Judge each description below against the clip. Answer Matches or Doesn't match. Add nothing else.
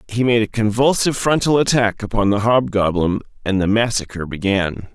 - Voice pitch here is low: Matches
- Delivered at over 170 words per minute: Doesn't match